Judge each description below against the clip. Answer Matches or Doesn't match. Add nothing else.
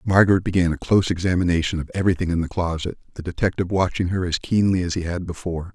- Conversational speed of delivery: Doesn't match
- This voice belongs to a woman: Doesn't match